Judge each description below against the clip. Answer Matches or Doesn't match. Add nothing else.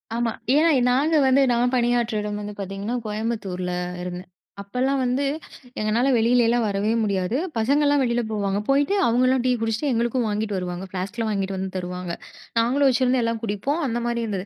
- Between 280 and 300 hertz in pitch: Doesn't match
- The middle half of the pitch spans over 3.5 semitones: Matches